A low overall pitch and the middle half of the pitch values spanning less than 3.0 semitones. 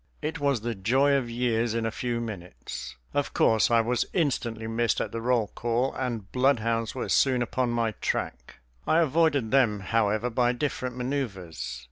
Yes: low, 120 Hz; narrow, 2.6 semitones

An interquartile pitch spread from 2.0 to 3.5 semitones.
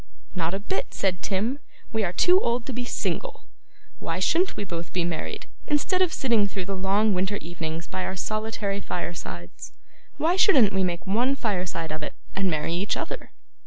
No: average, 5.1 semitones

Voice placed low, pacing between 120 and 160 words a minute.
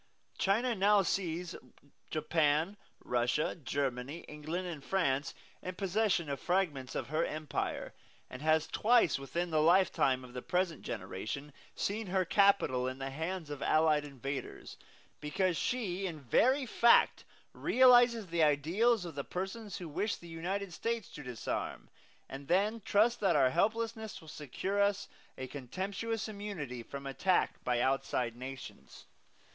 No: medium, 170 Hz; average, 140 wpm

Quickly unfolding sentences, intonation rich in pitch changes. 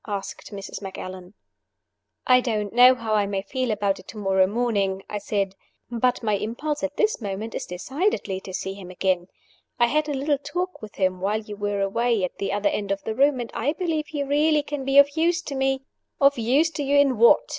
Yes: fast, 220 wpm; wide, 6.1 semitones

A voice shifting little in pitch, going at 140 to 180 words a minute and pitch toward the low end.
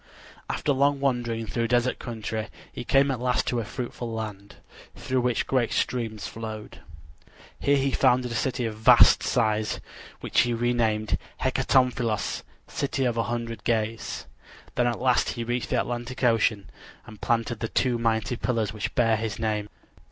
Yes: narrow, 2.1 semitones; average, 160 wpm; low, 120 Hz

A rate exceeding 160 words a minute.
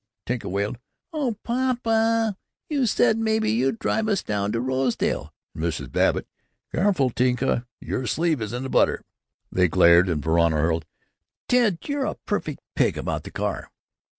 No: average, 155 wpm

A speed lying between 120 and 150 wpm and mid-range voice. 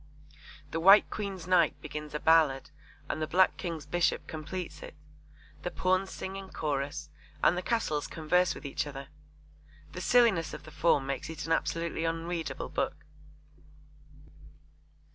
Yes: average, 145 wpm; medium, 165 Hz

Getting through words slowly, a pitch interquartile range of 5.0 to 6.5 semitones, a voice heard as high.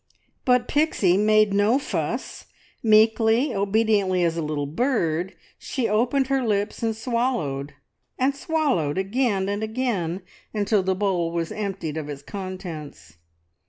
Yes: slow, 130 wpm; wide, 5.4 semitones; high, 205 Hz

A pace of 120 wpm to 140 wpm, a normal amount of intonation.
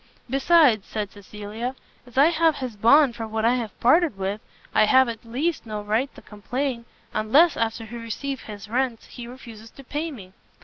No: average, 185 wpm; average, 4.0 semitones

